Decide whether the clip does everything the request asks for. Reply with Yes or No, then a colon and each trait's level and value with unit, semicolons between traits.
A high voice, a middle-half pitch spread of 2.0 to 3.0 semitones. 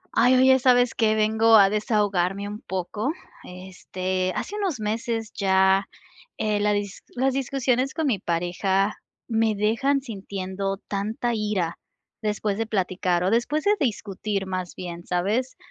No: high, 210 Hz; average, 3.7 semitones